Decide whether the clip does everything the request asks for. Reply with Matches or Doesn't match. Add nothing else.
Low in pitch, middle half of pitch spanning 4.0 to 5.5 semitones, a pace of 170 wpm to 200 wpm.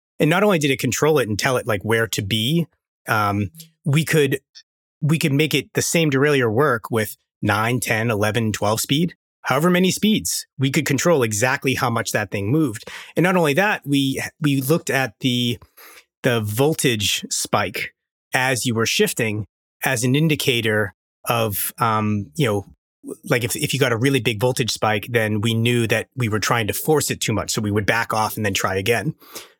Matches